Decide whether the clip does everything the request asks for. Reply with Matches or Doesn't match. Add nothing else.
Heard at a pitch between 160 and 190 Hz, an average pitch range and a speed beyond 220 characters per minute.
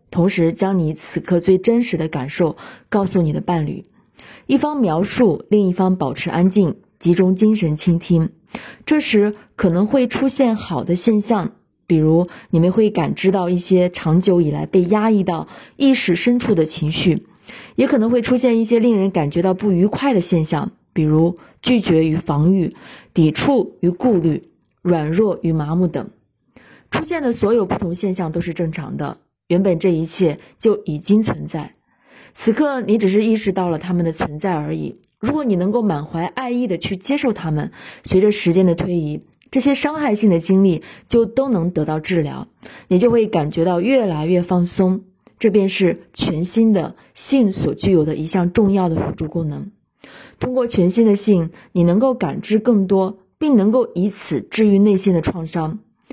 Matches